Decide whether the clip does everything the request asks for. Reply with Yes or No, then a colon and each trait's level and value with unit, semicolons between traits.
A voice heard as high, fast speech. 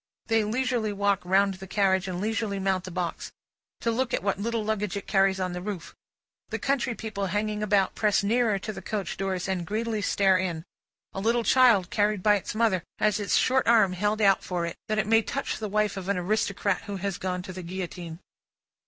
Yes: high, 200 Hz; fast, 215 wpm